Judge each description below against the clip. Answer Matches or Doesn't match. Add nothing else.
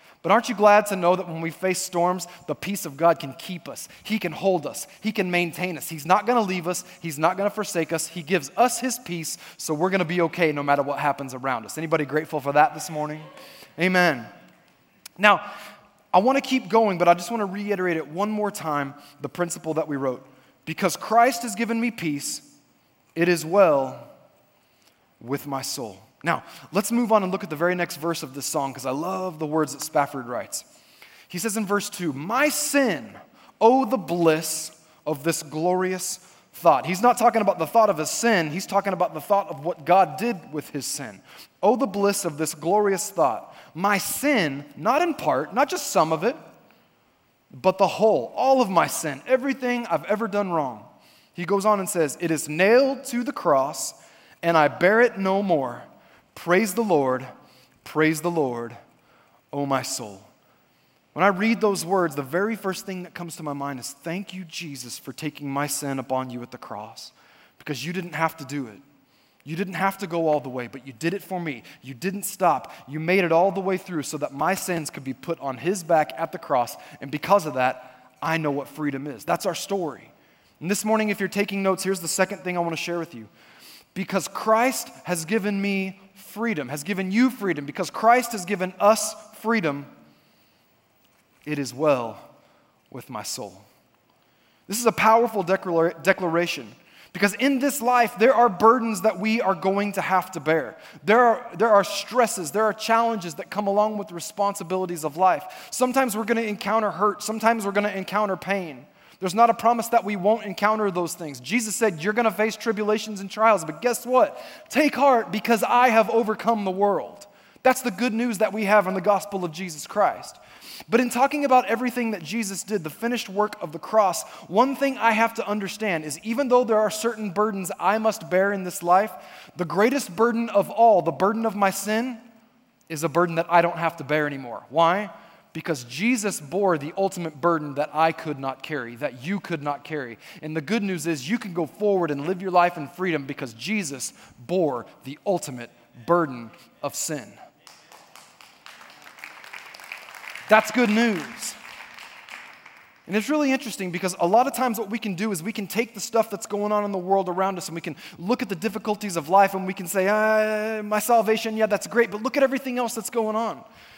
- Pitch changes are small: Doesn't match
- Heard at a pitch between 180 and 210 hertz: Matches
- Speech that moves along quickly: Matches